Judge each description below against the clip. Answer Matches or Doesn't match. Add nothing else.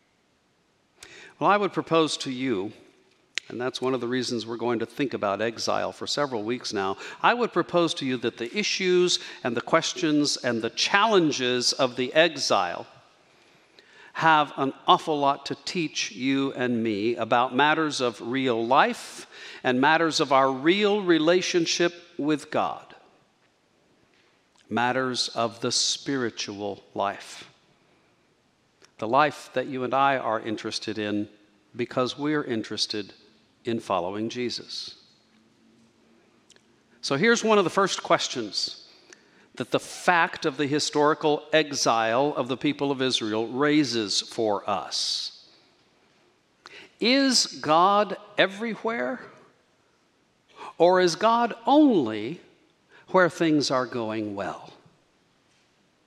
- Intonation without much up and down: Doesn't match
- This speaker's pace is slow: Matches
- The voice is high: Doesn't match